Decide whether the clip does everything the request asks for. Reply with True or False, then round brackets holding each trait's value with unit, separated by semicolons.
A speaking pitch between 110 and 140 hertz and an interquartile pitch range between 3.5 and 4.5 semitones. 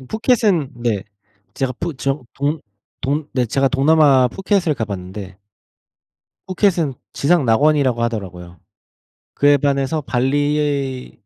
True (135 Hz; 3.9 semitones)